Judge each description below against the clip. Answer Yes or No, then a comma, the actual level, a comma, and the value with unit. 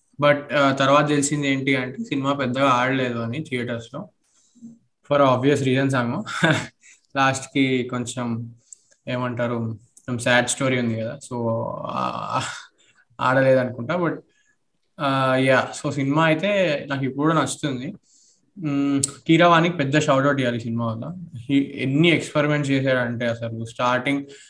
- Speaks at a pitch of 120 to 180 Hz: Yes, low, 135 Hz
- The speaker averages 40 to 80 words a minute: No, average, 110 wpm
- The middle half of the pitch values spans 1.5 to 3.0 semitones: Yes, average, 2.7 semitones